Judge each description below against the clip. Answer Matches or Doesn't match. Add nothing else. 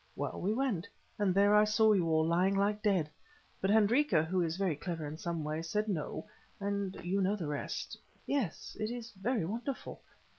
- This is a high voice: Matches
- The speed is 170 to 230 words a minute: Matches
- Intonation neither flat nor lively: Matches